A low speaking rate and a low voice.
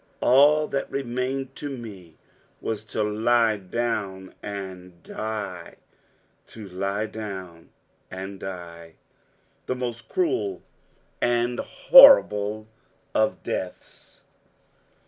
Yes: slow, 90 wpm; low, 110 Hz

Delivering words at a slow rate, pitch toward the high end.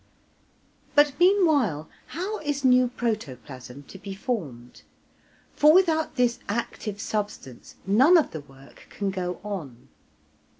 Yes: slow, 120 wpm; high, 210 Hz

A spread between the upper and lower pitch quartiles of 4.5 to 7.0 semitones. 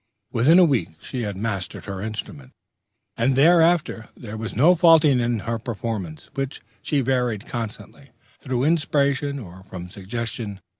Yes: wide, 5.4 semitones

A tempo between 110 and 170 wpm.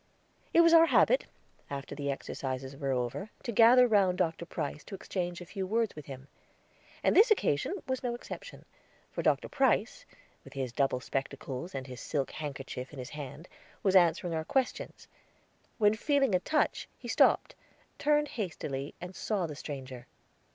Yes: average, 165 wpm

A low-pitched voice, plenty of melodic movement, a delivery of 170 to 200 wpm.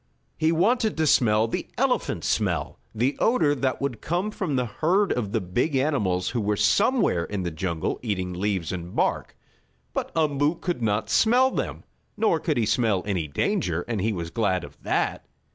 Yes: low, 115 Hz; wide, 8.9 semitones; average, 180 wpm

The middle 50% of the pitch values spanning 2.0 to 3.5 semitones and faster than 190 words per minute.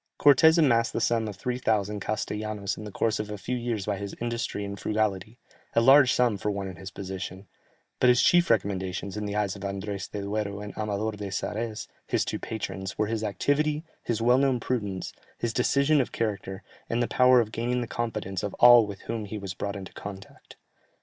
Yes: average, 3.0 semitones; fast, 205 wpm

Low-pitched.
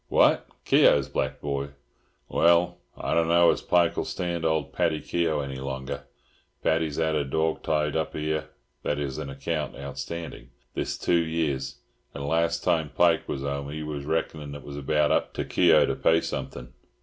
Yes: very low, 75 Hz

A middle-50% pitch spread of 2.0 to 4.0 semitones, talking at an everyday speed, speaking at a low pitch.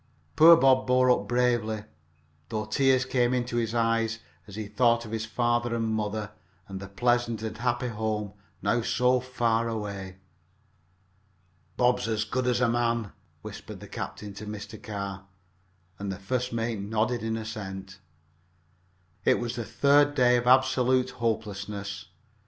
Yes: narrow, 2.6 semitones; average, 150 wpm; low, 115 Hz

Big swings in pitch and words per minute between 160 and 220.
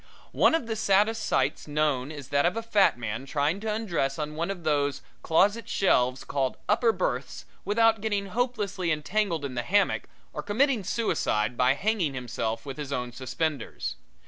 Yes: wide, 7.7 semitones; average, 170 wpm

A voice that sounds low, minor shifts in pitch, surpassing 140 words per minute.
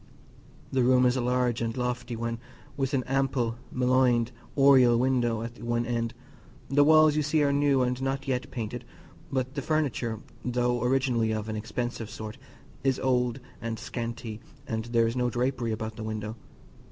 Yes: low, 125 Hz; narrow, 2.2 semitones; average, 170 wpm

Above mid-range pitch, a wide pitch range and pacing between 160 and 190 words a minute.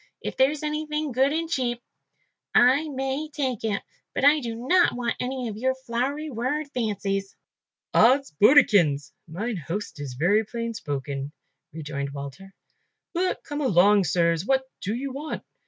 No: high, 235 Hz; wide, 6.6 semitones; average, 150 wpm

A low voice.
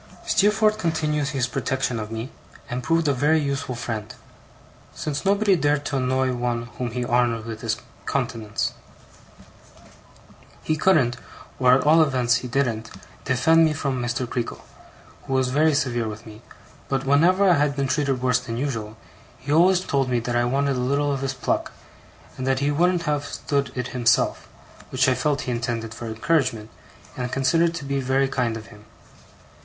Yes: low, 130 Hz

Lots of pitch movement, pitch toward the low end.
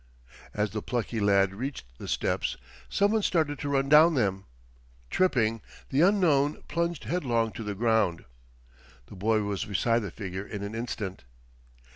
Yes: wide, 6.0 semitones; low, 115 Hz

